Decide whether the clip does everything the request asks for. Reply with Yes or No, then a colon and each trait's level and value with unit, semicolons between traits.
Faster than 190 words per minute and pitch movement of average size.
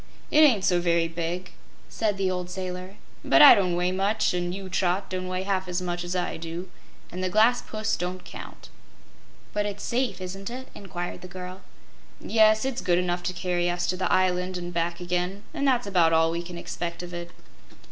No: fast, 205 wpm; narrow, 1.9 semitones